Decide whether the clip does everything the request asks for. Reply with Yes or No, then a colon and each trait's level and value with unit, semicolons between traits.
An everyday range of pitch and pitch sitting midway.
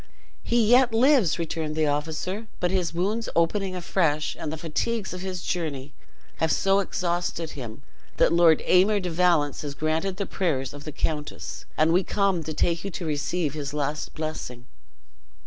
Yes: average, 3.7 semitones; medium, 170 Hz